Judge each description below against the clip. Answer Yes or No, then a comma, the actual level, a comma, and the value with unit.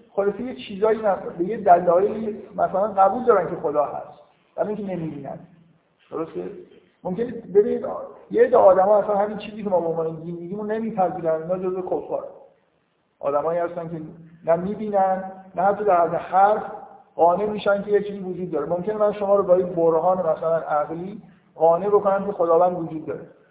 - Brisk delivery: Yes, fast, 175 wpm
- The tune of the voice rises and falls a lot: No, average, 3.3 semitones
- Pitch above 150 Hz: Yes, high, 190 Hz